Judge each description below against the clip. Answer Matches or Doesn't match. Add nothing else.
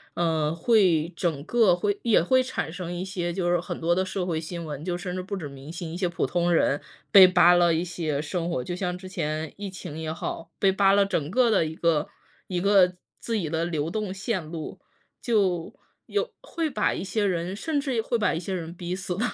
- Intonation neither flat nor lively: Matches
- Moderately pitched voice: Matches